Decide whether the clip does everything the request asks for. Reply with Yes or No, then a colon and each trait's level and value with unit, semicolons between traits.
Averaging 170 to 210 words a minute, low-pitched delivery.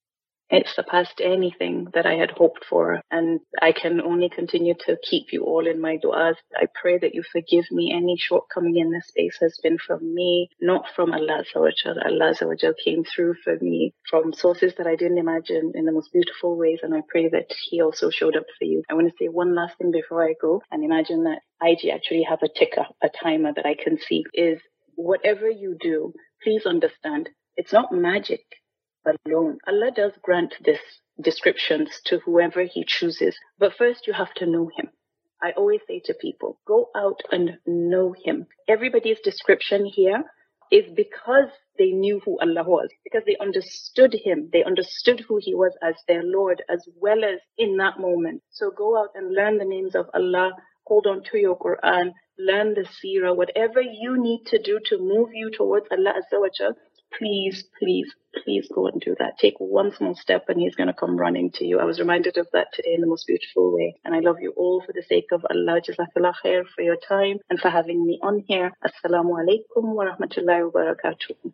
No: average, 195 wpm; high, 190 Hz